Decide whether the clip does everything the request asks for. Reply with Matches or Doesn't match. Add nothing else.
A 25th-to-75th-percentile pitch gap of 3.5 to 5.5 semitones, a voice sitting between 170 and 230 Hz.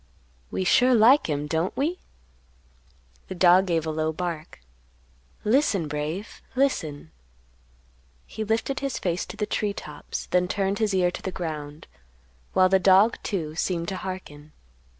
Matches